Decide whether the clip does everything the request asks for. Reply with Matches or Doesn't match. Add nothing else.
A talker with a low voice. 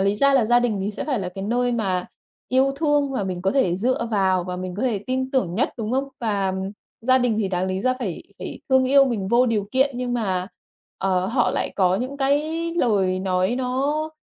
Doesn't match